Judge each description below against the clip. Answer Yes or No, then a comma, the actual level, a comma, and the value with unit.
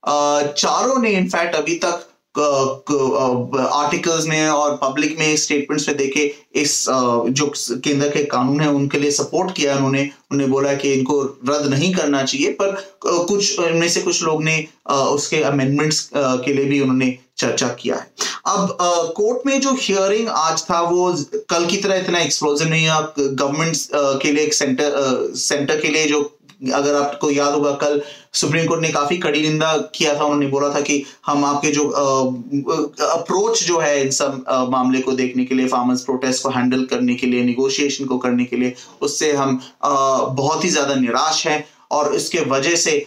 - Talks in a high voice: No, medium, 145 Hz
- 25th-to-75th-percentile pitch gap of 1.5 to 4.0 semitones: Yes, average, 2.7 semitones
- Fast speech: No, average, 175 wpm